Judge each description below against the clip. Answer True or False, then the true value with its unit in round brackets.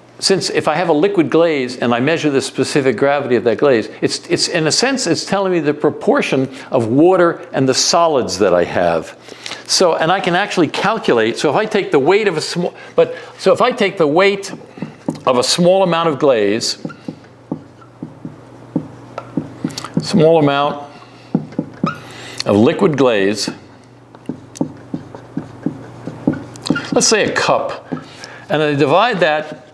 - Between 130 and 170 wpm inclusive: True (150 wpm)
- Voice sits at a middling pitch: True (155 Hz)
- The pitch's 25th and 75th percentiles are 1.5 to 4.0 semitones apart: False (5.6 semitones)